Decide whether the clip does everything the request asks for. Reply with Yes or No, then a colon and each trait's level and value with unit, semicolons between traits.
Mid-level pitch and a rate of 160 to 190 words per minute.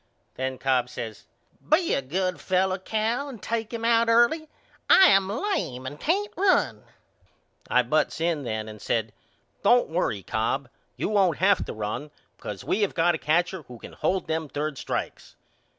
Yes: medium, 175 Hz; average, 170 wpm